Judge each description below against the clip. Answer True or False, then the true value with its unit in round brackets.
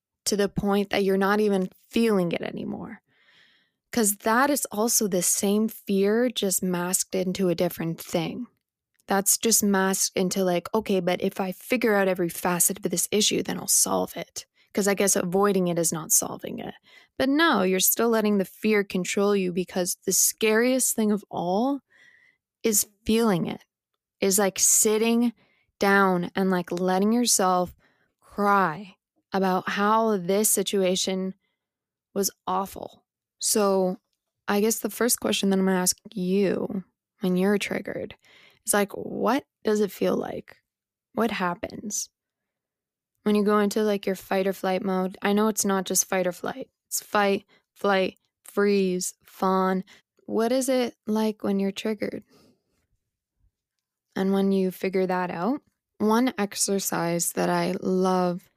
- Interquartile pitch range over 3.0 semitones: False (2.5 semitones)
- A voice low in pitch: False (200 Hz)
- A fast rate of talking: False (155 wpm)